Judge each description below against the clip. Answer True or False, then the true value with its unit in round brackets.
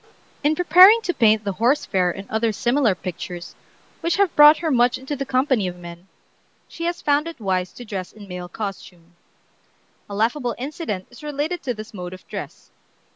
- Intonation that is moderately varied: False (7.8 semitones)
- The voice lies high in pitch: True (235 Hz)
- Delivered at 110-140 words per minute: False (185 wpm)